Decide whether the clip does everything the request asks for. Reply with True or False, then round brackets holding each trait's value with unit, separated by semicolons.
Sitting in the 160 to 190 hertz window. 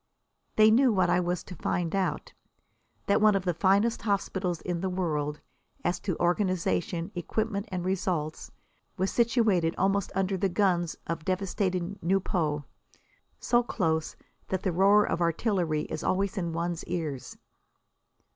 True (185 Hz)